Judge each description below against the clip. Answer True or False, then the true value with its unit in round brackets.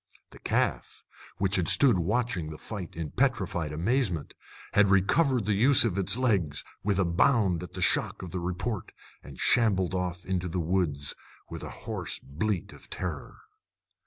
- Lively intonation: False (3.9 semitones)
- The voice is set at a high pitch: False (95 Hz)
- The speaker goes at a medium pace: True (165 wpm)